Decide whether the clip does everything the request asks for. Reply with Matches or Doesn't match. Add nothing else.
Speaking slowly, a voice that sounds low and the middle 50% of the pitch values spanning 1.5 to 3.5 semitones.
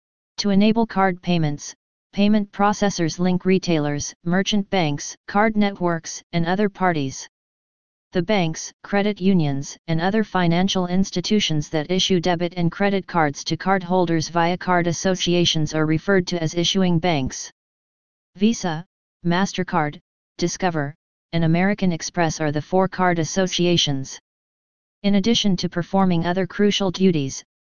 Doesn't match